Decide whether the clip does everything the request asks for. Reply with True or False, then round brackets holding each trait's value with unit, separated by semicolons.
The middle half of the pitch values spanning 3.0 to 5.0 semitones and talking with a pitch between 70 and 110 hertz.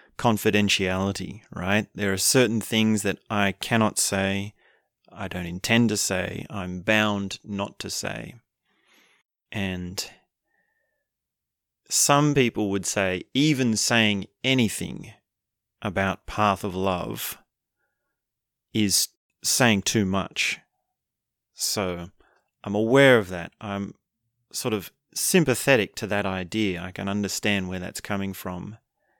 False (2.4 semitones; 100 Hz)